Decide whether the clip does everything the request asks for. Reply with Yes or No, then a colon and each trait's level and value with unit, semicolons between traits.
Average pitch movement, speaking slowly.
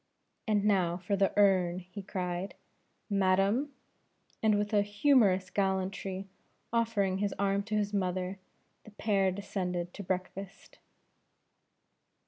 No: narrow, 1.7 semitones; slow, 115 wpm